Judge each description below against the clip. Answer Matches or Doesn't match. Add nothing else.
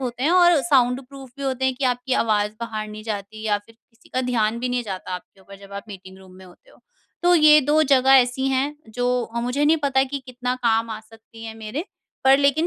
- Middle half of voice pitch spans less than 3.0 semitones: Doesn't match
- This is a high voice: Matches